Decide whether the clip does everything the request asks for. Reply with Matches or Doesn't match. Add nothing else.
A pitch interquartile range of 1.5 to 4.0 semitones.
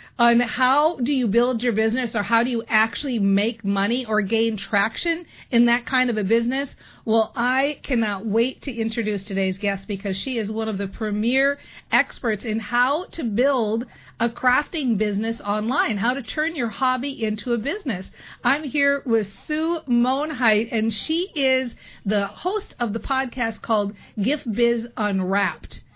Matches